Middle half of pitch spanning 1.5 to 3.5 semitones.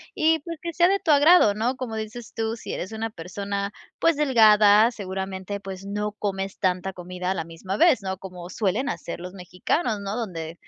No: average, 4.0 semitones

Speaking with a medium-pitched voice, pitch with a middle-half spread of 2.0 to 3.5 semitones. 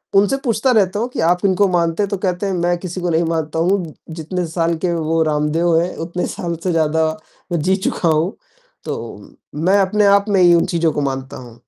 Yes: medium, 175 Hz; average, 2.9 semitones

